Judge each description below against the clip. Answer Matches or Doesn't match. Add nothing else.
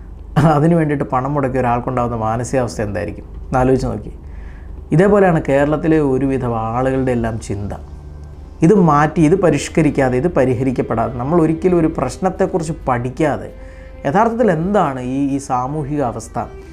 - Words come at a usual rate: Matches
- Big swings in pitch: Matches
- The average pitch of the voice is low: Matches